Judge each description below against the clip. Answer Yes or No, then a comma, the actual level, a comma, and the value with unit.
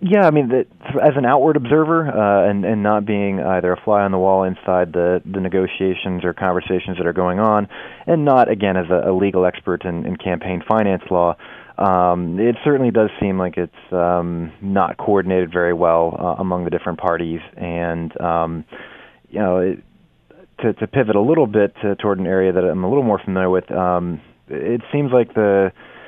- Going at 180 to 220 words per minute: Yes, average, 200 wpm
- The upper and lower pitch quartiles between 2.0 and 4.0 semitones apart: Yes, average, 2.9 semitones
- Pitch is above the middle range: No, very low, 95 Hz